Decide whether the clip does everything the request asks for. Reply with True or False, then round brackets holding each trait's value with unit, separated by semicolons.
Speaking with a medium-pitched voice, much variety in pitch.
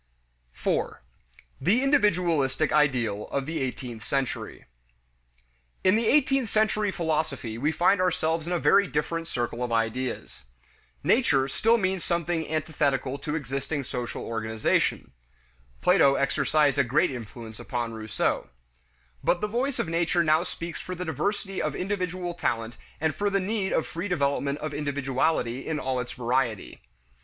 True (155 Hz; 5.8 semitones)